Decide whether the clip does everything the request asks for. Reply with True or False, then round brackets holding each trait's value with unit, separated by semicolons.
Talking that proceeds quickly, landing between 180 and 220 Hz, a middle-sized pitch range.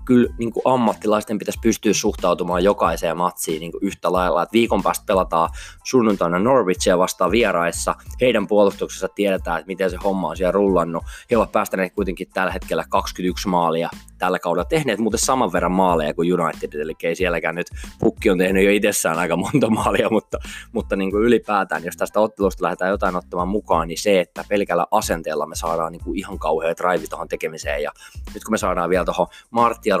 False (190 wpm; 95 Hz; 3.3 semitones)